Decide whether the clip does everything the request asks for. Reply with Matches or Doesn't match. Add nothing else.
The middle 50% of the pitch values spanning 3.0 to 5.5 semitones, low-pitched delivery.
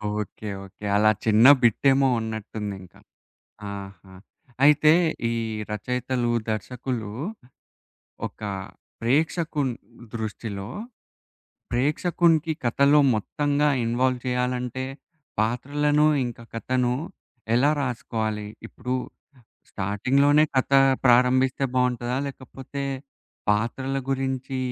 Matches